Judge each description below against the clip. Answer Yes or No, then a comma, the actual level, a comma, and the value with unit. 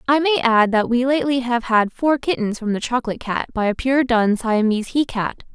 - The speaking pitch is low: No, high, 240 Hz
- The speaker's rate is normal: No, fast, 225 wpm